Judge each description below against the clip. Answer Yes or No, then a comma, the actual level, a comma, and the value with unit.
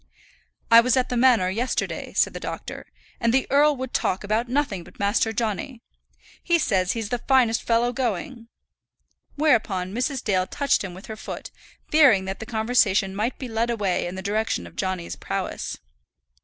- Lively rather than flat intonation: No, average, 4.2 semitones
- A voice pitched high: Yes, high, 225 Hz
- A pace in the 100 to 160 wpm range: No, average, 175 wpm